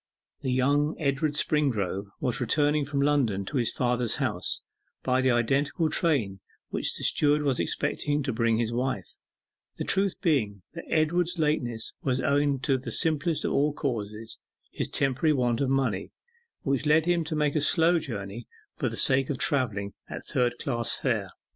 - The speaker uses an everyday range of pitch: Yes, average, 3.9 semitones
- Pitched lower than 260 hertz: Yes, low, 135 Hz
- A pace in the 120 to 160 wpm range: No, average, 170 wpm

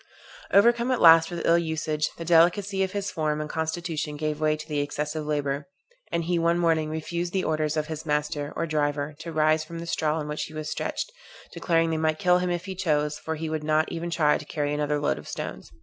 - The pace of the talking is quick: Yes, fast, 230 wpm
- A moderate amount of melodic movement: No, narrow, 2.0 semitones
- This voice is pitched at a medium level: Yes, medium, 155 Hz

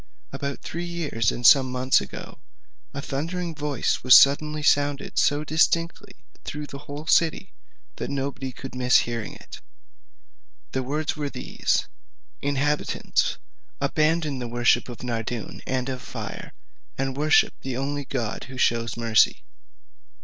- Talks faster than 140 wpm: No, slow, 135 wpm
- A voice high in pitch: No, medium, 140 Hz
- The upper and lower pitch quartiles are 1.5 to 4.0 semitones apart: Yes, average, 3.0 semitones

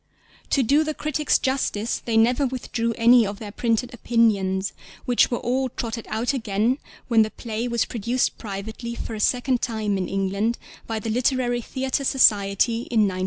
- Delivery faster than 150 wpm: Yes, average, 170 wpm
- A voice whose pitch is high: Yes, high, 230 Hz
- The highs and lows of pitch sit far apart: No, narrow, 2.6 semitones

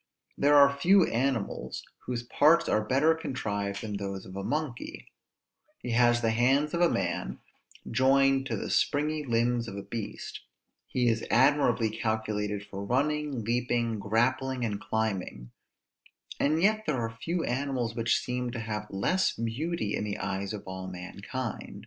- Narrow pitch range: No, average, 4.7 semitones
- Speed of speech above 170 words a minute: No, average, 155 wpm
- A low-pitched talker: Yes, low, 120 Hz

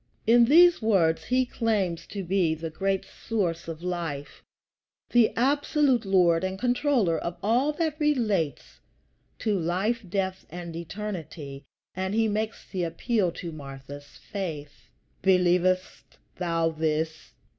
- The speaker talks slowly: Yes, slow, 125 wpm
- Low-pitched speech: No, medium, 185 Hz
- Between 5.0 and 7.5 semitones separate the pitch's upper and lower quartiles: Yes, average, 5.3 semitones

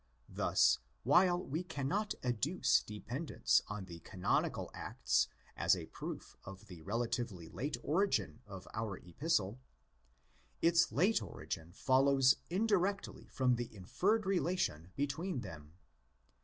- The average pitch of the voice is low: Yes, low, 130 Hz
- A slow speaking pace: Yes, slow, 115 wpm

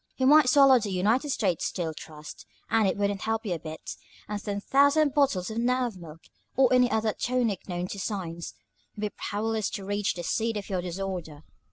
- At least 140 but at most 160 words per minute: No, average, 200 wpm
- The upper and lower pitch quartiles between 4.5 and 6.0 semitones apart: Yes, average, 5.1 semitones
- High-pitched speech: Yes, high, 205 Hz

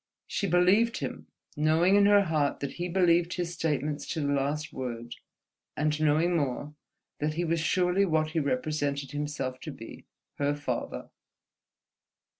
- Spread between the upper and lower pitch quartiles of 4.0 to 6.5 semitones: No, average, 3.4 semitones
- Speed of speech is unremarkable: Yes, average, 150 wpm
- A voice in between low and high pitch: Yes, medium, 155 Hz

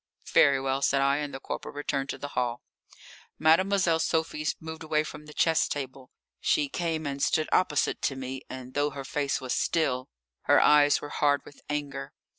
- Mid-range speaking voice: Yes, medium, 145 Hz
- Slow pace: No, average, 185 wpm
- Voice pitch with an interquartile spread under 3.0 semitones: Yes, narrow, 2.4 semitones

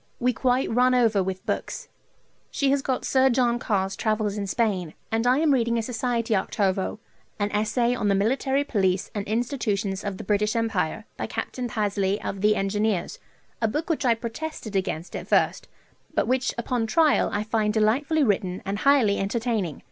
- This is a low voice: No, high, 220 Hz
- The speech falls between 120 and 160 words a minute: No, average, 180 wpm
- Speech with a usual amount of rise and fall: Yes, average, 3.7 semitones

